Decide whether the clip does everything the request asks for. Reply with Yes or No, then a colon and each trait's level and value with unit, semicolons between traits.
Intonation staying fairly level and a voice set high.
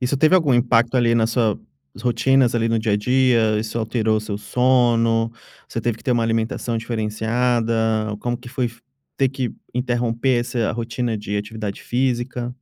No: narrow, 1.8 semitones; low, 120 Hz